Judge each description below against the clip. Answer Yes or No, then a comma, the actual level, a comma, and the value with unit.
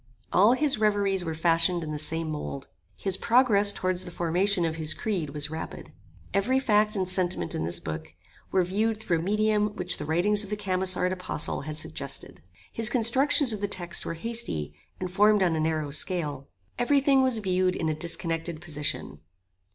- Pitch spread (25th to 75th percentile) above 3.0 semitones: Yes, average, 4.6 semitones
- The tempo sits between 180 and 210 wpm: Yes, average, 185 wpm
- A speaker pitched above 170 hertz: Yes, medium, 185 Hz